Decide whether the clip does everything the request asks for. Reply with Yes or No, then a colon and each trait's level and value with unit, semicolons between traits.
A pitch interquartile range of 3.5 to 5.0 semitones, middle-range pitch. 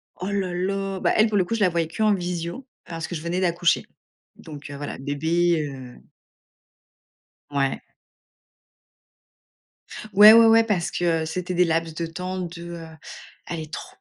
No: narrow, 2.6 semitones; medium, 175 Hz